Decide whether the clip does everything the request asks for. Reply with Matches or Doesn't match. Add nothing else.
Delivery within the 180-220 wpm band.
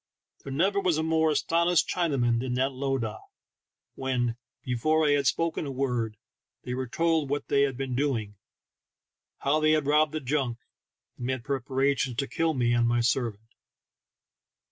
Doesn't match